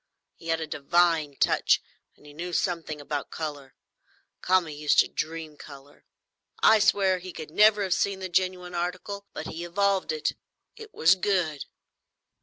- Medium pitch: Yes, medium, 175 Hz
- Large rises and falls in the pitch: No, average, 3.4 semitones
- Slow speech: No, average, 165 wpm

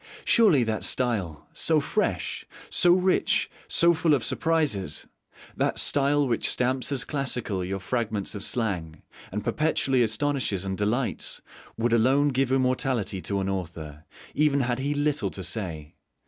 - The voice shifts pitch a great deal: Yes, wide, 6.6 semitones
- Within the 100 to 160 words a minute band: Yes, average, 145 wpm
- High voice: No, low, 120 Hz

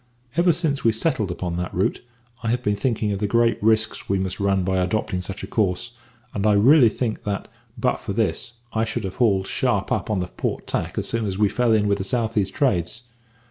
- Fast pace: Yes, fast, 230 wpm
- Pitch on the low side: Yes, low, 105 Hz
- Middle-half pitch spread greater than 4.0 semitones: No, average, 3.4 semitones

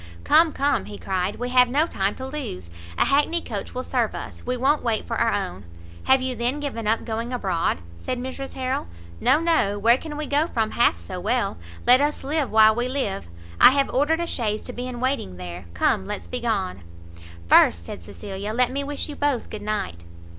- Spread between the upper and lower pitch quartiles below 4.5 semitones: No, average, 5.1 semitones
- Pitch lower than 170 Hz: No, high, 245 Hz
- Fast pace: Yes, fast, 210 wpm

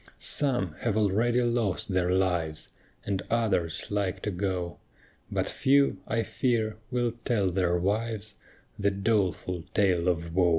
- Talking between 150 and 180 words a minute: No, slow, 135 wpm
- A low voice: Yes, low, 100 Hz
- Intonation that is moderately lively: Yes, average, 4.1 semitones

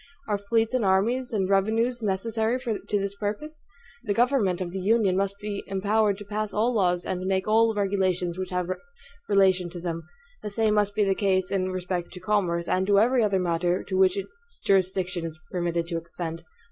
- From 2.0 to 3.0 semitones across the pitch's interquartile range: Yes, average, 2.7 semitones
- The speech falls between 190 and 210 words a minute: Yes, average, 195 wpm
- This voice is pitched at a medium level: No, high, 195 Hz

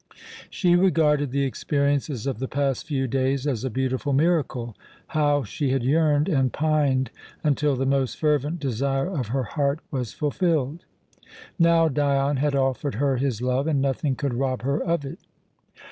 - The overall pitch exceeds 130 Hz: Yes, medium, 140 Hz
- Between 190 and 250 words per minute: No, average, 160 wpm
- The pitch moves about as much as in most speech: No, narrow, 2.2 semitones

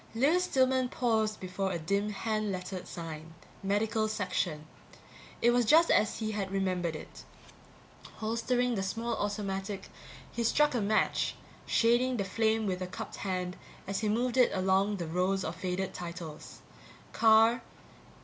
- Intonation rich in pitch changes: No, average, 3.7 semitones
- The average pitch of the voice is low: No, high, 205 Hz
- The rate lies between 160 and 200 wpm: No, average, 150 wpm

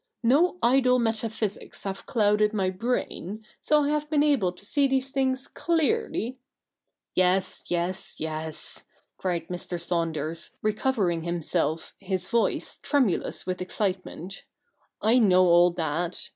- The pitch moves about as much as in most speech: No, wide, 6.2 semitones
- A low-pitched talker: No, high, 195 Hz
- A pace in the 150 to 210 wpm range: No, slow, 135 wpm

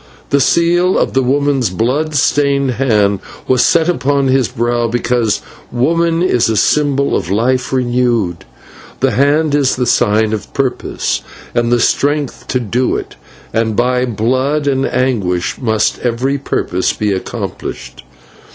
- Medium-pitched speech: No, low, 125 Hz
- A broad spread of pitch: No, average, 3.6 semitones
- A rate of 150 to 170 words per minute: No, average, 140 wpm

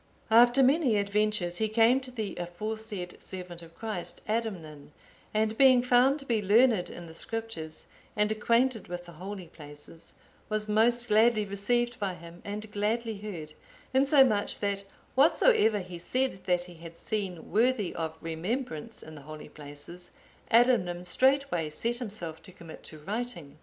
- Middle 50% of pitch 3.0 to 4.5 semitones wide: No, average, 5.2 semitones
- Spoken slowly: No, average, 150 wpm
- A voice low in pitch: No, high, 210 Hz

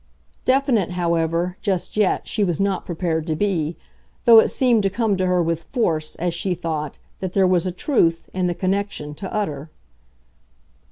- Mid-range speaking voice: Yes, medium, 180 Hz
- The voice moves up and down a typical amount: Yes, average, 3.3 semitones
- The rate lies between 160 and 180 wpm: Yes, average, 175 wpm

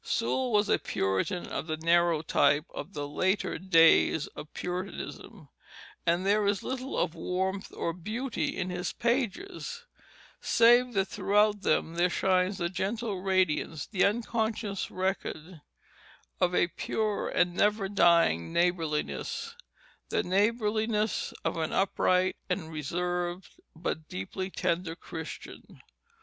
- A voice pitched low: No, medium, 185 Hz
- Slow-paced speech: Yes, slow, 125 wpm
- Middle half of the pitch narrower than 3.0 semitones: No, average, 3.8 semitones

